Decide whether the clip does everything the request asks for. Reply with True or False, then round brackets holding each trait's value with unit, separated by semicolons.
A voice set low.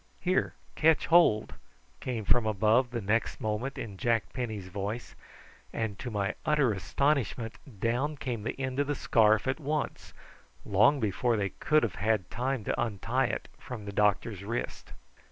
True (115 Hz)